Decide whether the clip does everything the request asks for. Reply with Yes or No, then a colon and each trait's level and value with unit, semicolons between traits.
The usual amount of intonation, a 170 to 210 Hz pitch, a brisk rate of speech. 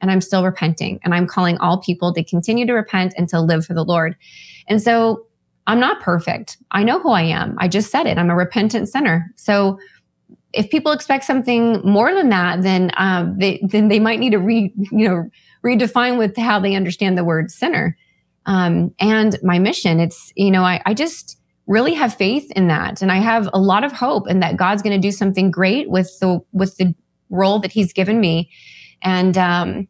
Yes: average, 3.4 semitones; high, 190 Hz; fast, 210 wpm